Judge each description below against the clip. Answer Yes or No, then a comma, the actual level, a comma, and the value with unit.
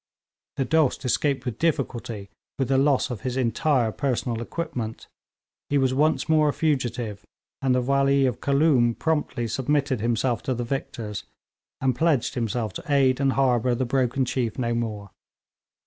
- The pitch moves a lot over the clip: No, average, 2.8 semitones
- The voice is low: Yes, low, 130 Hz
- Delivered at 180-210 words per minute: No, average, 160 wpm